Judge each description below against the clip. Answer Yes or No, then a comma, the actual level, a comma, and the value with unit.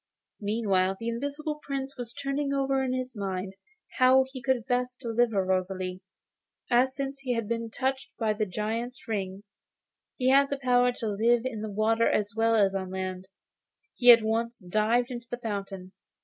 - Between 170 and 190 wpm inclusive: Yes, average, 175 wpm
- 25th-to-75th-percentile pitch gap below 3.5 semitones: No, average, 3.9 semitones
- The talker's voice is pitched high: Yes, high, 230 Hz